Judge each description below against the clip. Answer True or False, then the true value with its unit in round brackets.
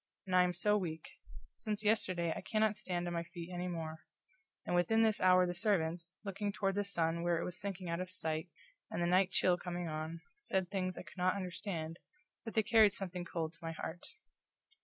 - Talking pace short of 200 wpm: False (205 wpm)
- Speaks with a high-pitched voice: False (180 Hz)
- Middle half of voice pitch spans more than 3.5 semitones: False (2.8 semitones)